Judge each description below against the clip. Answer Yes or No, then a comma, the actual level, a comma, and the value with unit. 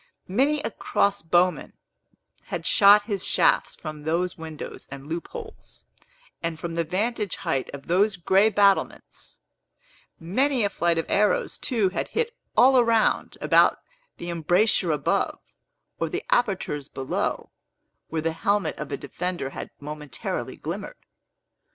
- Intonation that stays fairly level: No, average, 4.6 semitones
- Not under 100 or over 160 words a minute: Yes, slow, 135 wpm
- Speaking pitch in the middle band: Yes, medium, 180 Hz